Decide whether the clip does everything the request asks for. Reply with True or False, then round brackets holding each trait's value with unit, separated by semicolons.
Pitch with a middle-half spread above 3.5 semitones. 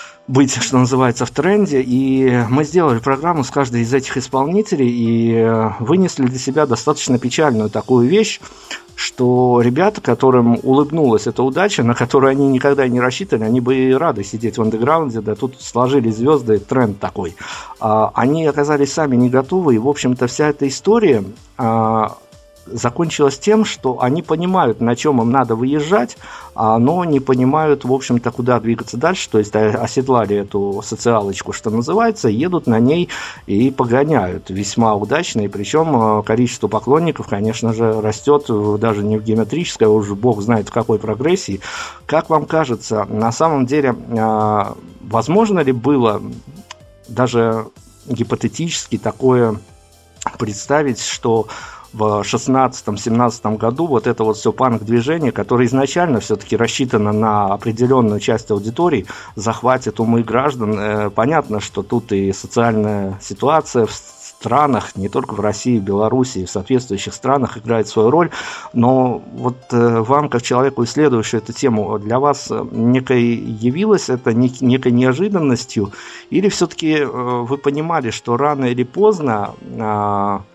True (3.9 semitones)